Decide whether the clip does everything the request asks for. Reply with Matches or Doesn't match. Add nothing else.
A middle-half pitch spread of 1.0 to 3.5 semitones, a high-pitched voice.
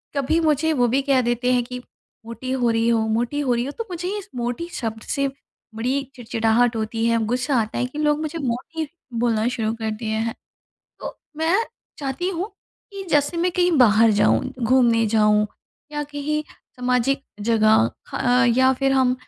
Doesn't match